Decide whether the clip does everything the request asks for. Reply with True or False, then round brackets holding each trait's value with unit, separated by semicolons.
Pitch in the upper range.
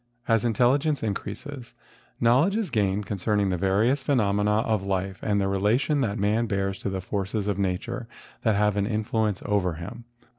False (105 Hz)